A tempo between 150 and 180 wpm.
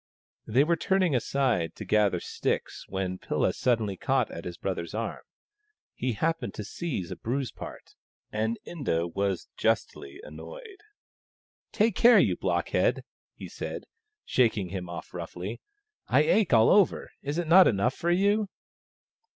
Yes: average, 155 wpm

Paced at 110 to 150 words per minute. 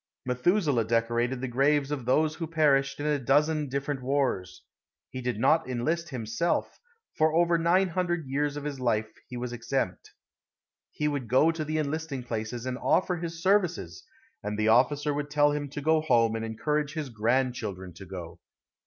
No: average, 175 wpm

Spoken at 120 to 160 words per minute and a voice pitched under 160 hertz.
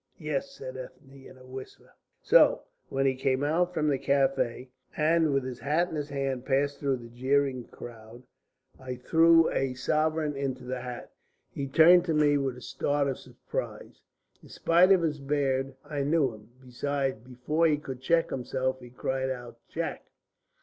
No: average, 175 wpm; low, 135 Hz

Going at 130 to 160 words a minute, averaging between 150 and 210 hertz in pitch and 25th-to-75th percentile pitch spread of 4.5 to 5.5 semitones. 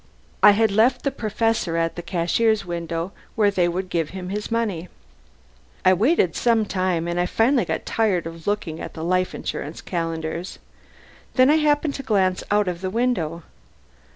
No: average, 175 wpm; medium, 185 Hz; average, 4.8 semitones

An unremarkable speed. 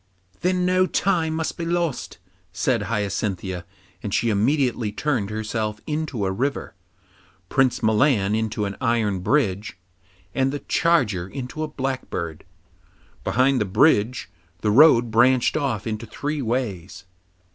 No: slow, 130 wpm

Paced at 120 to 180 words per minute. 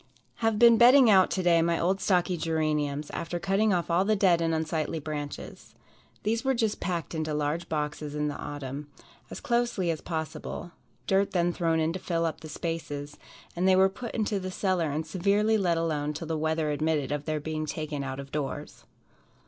No: average, 195 wpm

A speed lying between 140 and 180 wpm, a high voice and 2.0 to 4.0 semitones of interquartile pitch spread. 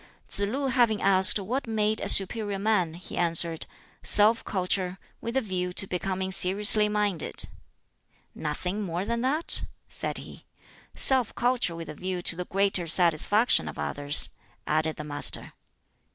Yes: average, 150 wpm; high, 195 Hz; average, 3.7 semitones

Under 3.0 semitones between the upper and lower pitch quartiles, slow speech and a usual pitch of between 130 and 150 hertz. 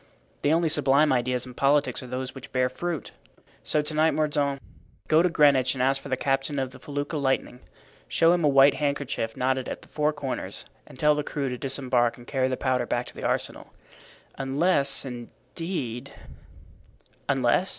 No: narrow, 2.6 semitones; average, 180 wpm; low, 135 Hz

